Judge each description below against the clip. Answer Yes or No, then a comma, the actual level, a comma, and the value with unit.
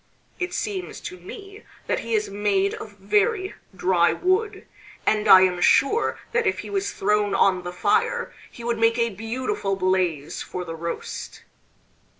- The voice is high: Yes, high, 210 Hz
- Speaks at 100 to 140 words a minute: No, average, 160 wpm